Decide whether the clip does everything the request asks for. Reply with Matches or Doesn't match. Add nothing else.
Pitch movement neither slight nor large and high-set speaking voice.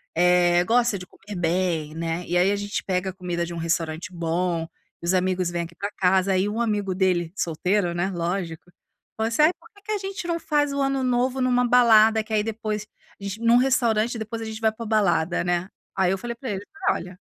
Matches